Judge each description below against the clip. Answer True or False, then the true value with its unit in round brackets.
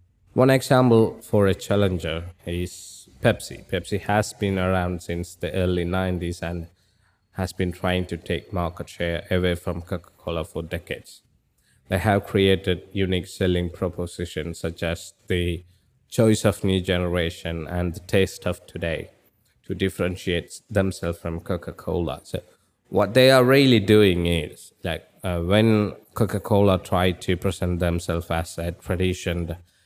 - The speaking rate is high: True (140 wpm)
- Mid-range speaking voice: False (90 Hz)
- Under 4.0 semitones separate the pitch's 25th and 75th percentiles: True (2.4 semitones)